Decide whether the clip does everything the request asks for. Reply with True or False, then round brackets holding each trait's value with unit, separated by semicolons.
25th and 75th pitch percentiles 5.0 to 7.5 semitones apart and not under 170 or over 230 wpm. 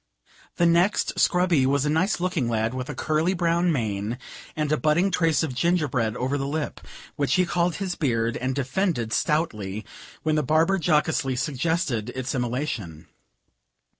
False (5.4 semitones; 160 wpm)